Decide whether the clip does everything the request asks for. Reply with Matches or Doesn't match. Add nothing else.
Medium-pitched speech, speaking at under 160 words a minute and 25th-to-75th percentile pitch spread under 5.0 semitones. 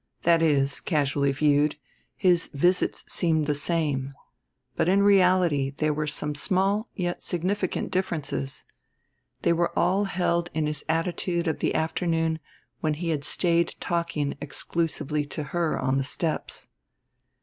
Matches